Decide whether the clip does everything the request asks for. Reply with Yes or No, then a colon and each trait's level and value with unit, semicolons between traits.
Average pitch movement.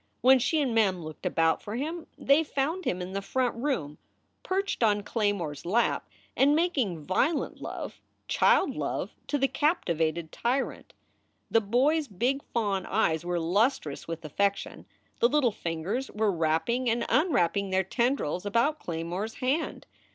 No: wide, 7.4 semitones